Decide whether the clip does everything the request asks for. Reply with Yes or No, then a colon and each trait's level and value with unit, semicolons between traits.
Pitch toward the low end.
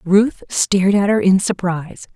No: high, 195 Hz